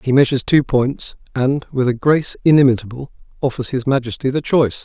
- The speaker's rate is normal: Yes, average, 175 wpm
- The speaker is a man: Yes, male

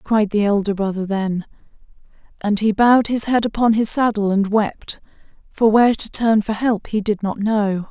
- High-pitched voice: Yes, high, 210 Hz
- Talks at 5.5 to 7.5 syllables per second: No, 4.9 syllables/s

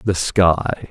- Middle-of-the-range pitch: No, very low, 85 Hz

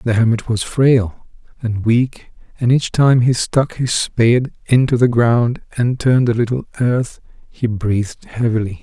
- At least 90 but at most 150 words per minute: No, average, 165 wpm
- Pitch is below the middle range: Yes, low, 120 Hz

